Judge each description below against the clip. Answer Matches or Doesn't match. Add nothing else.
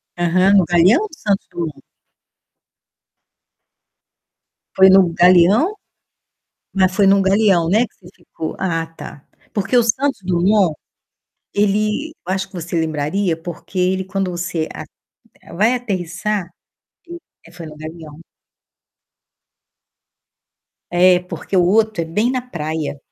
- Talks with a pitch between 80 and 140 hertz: Doesn't match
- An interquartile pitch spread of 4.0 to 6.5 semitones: Doesn't match